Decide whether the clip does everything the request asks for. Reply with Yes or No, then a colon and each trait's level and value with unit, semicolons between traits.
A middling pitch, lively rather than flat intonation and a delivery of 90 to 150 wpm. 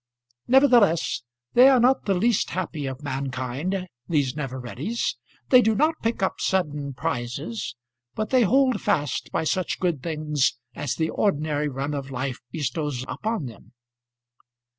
Yes: medium, 155 Hz; wide, 7.8 semitones; average, 145 wpm